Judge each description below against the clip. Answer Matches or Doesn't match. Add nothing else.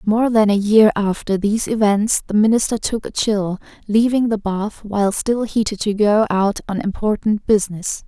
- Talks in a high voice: Matches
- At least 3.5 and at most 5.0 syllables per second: Matches